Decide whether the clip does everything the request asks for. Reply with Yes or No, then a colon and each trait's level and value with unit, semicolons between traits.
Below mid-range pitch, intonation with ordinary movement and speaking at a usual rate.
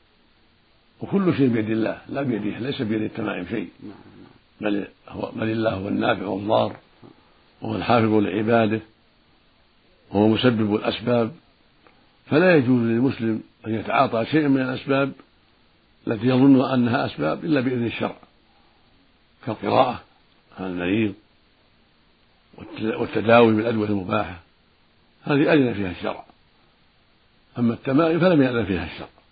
Yes: low, 115 Hz; average, 3.3 semitones; average, 110 wpm